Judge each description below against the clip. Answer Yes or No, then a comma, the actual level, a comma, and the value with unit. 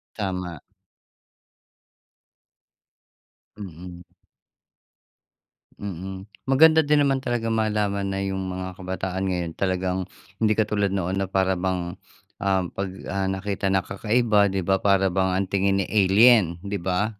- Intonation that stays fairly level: Yes, narrow, 1.9 semitones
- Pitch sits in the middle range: No, very low, 95 Hz